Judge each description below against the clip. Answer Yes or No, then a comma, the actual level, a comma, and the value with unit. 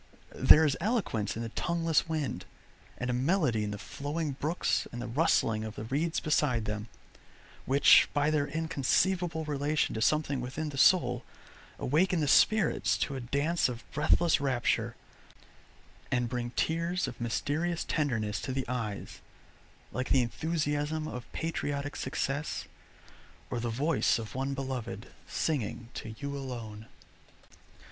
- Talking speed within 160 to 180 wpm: No, average, 140 wpm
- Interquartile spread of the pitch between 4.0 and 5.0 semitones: Yes, average, 4.7 semitones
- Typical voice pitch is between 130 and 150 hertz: Yes, medium, 140 Hz